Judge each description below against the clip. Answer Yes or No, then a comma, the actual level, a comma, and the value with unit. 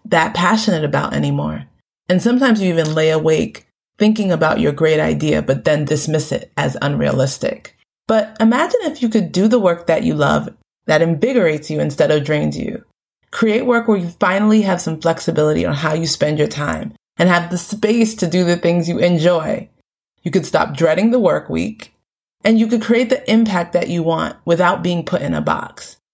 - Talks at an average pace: Yes, average, 195 wpm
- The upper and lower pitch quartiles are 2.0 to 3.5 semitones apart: No, wide, 5.6 semitones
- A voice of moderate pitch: Yes, medium, 175 Hz